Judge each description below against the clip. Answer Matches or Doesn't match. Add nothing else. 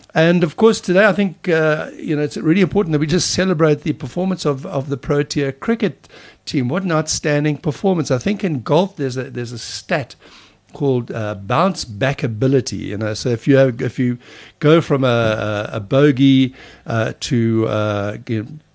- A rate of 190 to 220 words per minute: Matches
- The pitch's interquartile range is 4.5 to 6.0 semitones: Matches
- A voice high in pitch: Doesn't match